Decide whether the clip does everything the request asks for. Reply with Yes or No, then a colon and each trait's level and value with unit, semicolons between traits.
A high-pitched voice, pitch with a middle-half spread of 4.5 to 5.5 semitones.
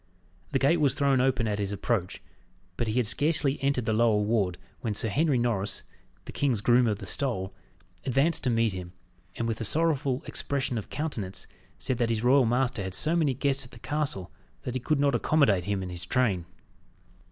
No: low, 120 Hz; average, 4.9 semitones